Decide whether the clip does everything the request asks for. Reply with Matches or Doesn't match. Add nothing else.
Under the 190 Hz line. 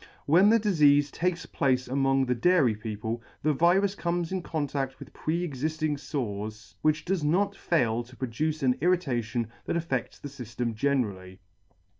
Matches